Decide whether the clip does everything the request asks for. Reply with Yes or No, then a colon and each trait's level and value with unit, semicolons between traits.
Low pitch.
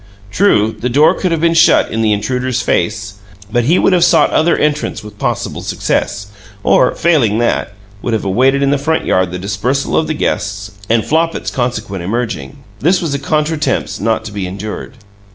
Yes: low, 120 Hz